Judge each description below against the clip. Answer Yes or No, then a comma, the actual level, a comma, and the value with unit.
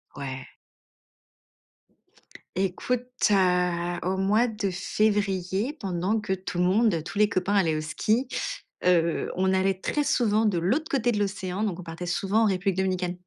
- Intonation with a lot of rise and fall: No, average, 2.9 semitones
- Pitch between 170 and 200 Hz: Yes, high, 190 Hz